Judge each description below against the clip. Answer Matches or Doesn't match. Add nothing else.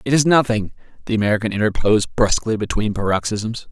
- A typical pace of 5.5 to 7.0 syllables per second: Matches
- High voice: Doesn't match